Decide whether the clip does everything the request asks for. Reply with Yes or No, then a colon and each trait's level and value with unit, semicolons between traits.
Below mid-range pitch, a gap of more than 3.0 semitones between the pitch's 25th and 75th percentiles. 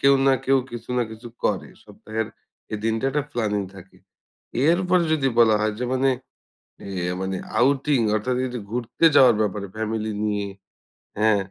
Yes: low, 115 Hz; average, 3.8 semitones